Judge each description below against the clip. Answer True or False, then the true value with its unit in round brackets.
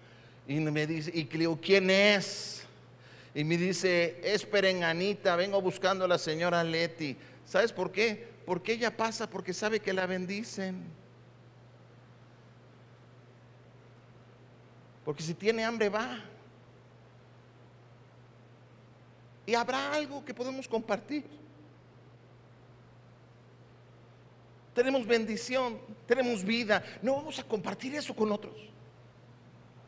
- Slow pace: True (100 wpm)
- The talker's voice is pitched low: False (165 Hz)